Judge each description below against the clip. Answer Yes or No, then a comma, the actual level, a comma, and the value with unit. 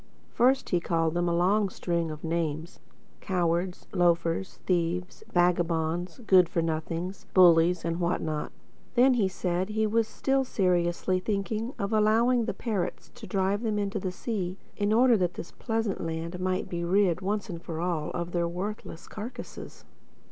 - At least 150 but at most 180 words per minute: Yes, average, 160 wpm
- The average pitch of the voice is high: No, medium, 180 Hz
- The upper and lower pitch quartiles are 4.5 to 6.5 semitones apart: No, average, 3.5 semitones